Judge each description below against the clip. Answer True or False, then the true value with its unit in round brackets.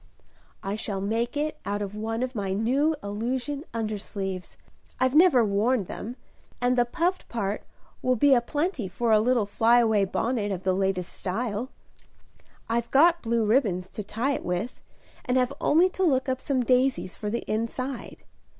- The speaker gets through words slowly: False (170 wpm)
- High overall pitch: True (235 Hz)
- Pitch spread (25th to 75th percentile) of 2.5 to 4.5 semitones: True (4.0 semitones)